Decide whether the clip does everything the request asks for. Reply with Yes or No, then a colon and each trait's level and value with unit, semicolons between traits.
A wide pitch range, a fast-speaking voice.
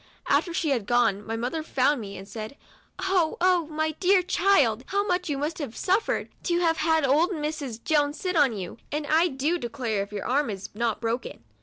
Yes: wide, 6.4 semitones; fast, 210 wpm